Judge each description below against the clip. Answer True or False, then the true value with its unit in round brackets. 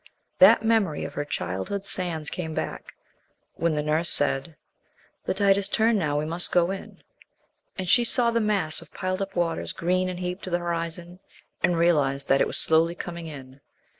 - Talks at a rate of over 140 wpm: True (190 wpm)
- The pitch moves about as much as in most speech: True (3.3 semitones)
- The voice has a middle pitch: True (170 Hz)